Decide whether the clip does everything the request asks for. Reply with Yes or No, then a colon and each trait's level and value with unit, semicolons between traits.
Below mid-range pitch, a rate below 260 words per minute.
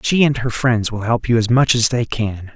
No: low, 115 Hz; fast, 280 wpm